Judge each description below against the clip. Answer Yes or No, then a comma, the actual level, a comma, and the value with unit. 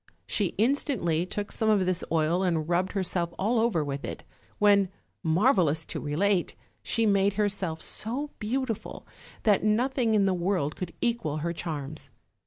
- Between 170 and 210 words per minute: No, average, 155 wpm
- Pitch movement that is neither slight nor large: Yes, average, 4.5 semitones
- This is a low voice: No, high, 190 Hz